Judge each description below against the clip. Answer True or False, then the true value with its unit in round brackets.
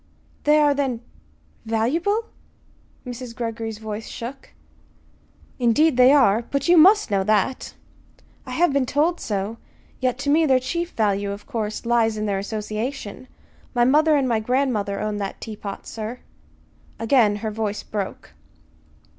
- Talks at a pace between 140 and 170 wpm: True (145 wpm)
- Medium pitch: False (235 Hz)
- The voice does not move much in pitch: False (4.7 semitones)